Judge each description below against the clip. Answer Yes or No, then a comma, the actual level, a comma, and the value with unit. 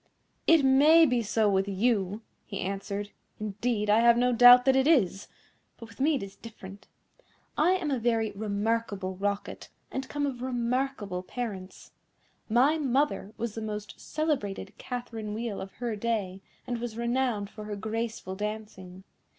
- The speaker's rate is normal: Yes, average, 160 wpm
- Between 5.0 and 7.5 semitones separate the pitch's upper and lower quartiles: No, average, 3.5 semitones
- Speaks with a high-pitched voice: Yes, high, 225 Hz